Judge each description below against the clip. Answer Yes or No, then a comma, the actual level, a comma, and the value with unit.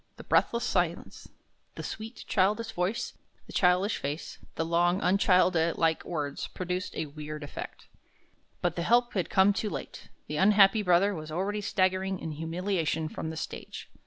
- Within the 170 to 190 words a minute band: No, average, 155 wpm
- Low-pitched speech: No, medium, 180 Hz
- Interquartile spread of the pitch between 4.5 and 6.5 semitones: No, average, 3.6 semitones